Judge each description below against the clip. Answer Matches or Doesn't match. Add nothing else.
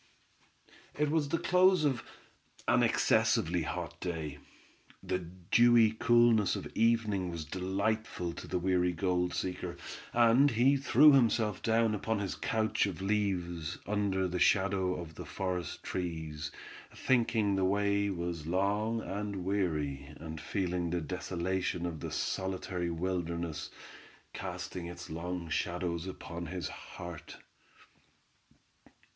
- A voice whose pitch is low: Matches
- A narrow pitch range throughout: Doesn't match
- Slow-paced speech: Matches